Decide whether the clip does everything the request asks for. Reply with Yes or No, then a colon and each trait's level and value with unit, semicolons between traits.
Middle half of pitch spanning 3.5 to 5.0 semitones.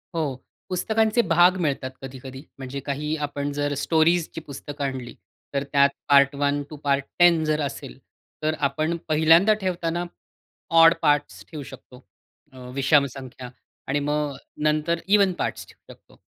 No: average, 3.0 semitones